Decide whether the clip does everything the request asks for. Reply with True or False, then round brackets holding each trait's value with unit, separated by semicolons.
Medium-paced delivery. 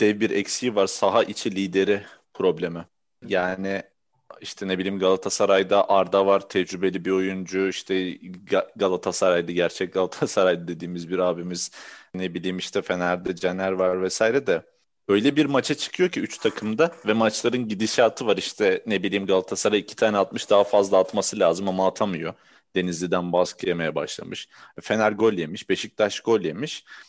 False (150 wpm)